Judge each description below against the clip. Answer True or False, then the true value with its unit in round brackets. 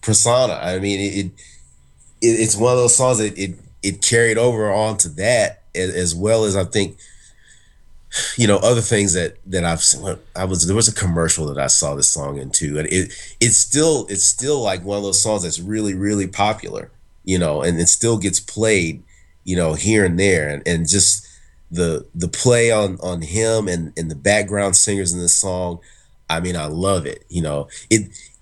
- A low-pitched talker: True (95 Hz)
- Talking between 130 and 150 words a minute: False (205 wpm)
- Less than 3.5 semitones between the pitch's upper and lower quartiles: False (4.0 semitones)